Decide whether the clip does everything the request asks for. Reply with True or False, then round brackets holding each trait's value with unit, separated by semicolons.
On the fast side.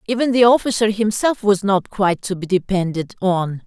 False (180 wpm)